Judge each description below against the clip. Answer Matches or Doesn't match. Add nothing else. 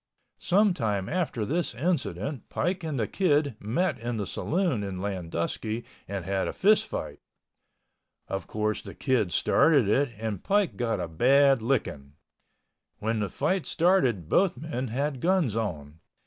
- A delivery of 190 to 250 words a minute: Doesn't match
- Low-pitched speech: Matches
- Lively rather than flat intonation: Matches